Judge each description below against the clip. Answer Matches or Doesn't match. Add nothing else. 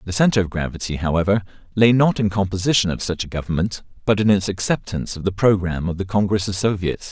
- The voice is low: Matches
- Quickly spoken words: Matches